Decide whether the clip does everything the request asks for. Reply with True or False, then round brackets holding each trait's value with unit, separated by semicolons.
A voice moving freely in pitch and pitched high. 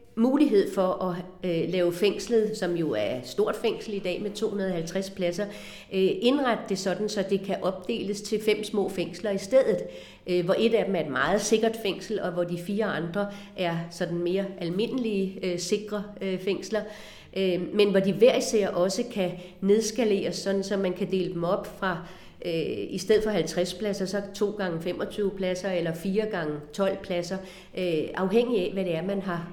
False (2.5 semitones; 195 Hz)